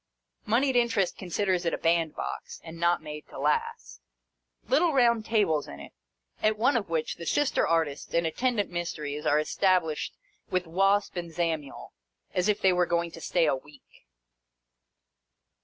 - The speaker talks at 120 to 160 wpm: Yes, average, 155 wpm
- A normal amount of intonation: Yes, average, 4.8 semitones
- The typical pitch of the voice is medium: Yes, medium, 175 Hz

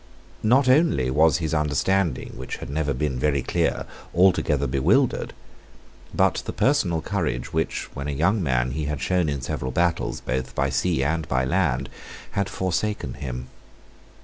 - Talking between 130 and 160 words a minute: Yes, average, 155 wpm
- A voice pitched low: Yes, very low, 75 Hz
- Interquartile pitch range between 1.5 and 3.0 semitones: No, average, 5.2 semitones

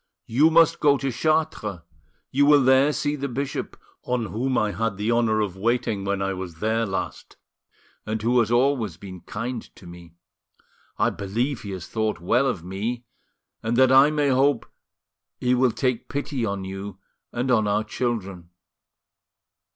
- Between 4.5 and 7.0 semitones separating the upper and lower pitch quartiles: Yes, average, 4.8 semitones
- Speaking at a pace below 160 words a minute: No, average, 165 wpm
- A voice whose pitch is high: No, low, 115 Hz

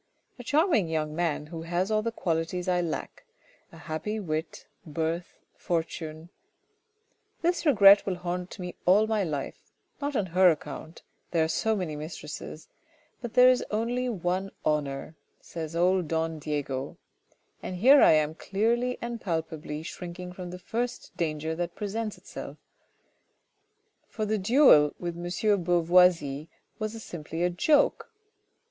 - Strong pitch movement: No, average, 4.9 semitones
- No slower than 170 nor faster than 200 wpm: No, average, 150 wpm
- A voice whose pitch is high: No, medium, 175 Hz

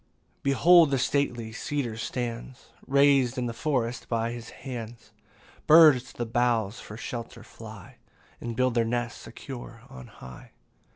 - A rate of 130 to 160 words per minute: Yes, average, 150 wpm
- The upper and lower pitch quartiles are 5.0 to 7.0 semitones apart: No, average, 2.7 semitones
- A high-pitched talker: No, low, 120 Hz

